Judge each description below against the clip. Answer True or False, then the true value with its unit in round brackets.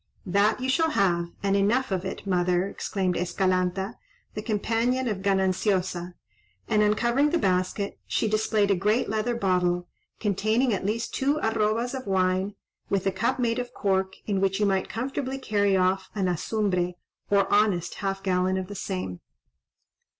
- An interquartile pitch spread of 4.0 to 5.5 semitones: False (3.0 semitones)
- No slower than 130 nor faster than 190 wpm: True (160 wpm)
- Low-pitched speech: False (200 Hz)